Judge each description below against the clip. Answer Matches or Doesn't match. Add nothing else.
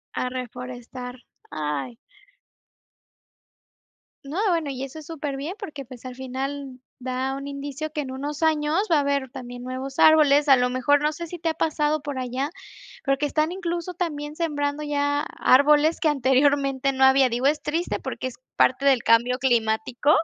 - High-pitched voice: Matches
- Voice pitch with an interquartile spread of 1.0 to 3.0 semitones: Matches